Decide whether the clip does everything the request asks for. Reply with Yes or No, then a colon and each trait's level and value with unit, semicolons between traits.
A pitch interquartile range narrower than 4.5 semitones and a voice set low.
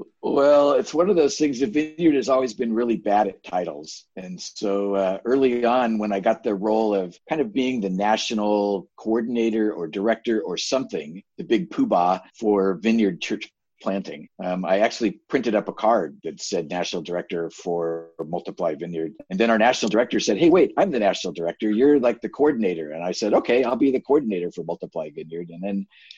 Yes: average, 4.0 semitones; low, 105 Hz